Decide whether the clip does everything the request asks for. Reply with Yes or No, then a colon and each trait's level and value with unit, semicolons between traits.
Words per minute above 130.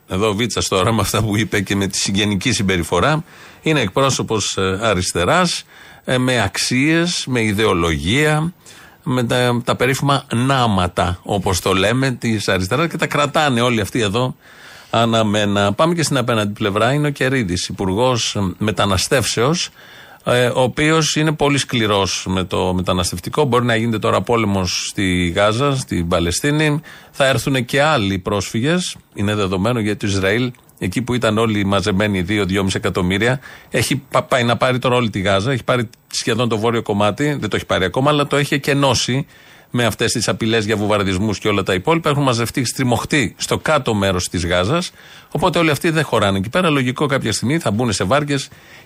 Yes: average, 165 wpm